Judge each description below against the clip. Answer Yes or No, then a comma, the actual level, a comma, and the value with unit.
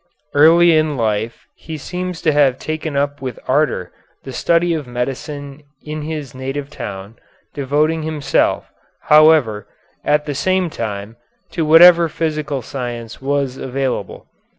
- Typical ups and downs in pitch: Yes, average, 3.4 semitones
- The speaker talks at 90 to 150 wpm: Yes, slow, 135 wpm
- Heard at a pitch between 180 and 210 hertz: No, medium, 145 Hz